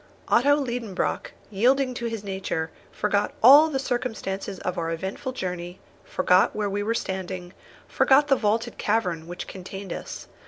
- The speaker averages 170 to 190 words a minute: No, average, 150 wpm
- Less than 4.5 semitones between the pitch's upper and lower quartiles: No, average, 4.8 semitones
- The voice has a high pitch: Yes, high, 205 Hz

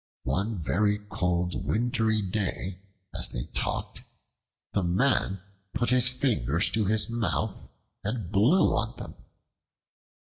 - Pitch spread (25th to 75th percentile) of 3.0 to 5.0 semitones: Yes, average, 3.9 semitones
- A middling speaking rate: No, slow, 115 wpm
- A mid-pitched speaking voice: No, low, 105 Hz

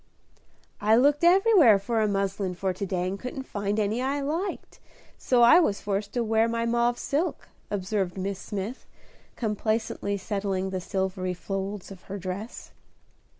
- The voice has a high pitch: Yes, high, 205 Hz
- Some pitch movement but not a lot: Yes, average, 3.6 semitones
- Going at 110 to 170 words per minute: Yes, average, 155 wpm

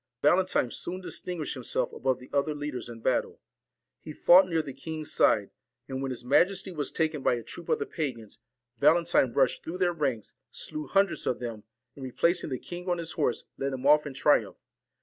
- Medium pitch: Yes, medium, 150 Hz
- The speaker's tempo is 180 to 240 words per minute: Yes, average, 200 wpm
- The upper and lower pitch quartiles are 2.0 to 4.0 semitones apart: No, average, 4.9 semitones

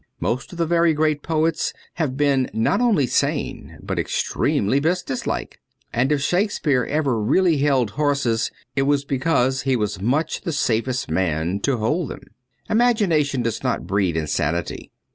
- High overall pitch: No, medium, 140 Hz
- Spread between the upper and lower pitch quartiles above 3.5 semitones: Yes, average, 5.3 semitones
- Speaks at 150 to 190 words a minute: Yes, average, 155 wpm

